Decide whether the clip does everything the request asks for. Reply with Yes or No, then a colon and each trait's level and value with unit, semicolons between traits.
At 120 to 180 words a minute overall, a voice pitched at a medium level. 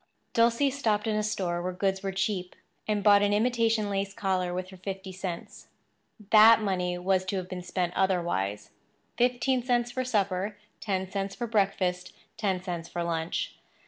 No: average, 165 wpm; high, 195 Hz